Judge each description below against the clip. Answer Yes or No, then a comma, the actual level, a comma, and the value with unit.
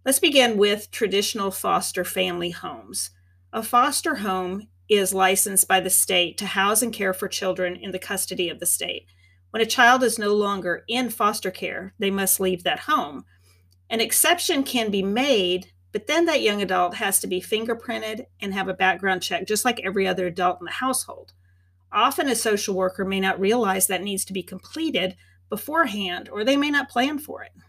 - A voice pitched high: Yes, high, 195 Hz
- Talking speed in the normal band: Yes, average, 190 wpm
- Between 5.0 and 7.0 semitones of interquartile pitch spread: No, average, 3.8 semitones